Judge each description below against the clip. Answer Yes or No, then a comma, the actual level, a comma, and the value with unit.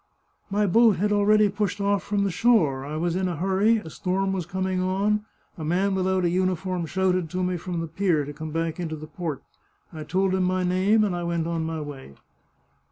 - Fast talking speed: Yes, fast, 225 wpm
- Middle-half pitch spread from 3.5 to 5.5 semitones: No, average, 2.9 semitones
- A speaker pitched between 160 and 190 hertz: Yes, medium, 185 Hz